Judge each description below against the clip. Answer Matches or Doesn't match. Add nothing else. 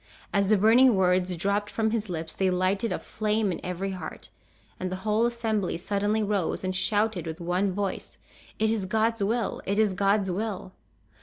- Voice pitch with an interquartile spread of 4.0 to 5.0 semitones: Doesn't match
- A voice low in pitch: Doesn't match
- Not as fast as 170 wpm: Doesn't match